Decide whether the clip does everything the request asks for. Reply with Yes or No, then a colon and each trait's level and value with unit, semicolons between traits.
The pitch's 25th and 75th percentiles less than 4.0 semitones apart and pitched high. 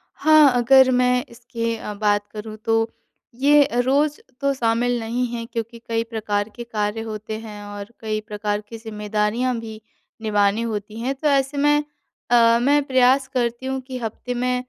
Yes: average, 2.9 semitones; high, 230 Hz